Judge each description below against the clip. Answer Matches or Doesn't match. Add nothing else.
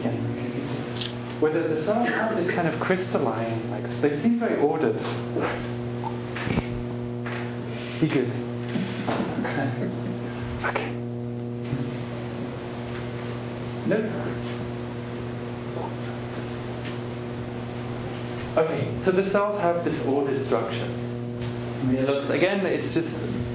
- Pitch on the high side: Doesn't match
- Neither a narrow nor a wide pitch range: Doesn't match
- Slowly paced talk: Matches